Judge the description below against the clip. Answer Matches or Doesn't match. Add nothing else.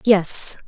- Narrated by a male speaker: Doesn't match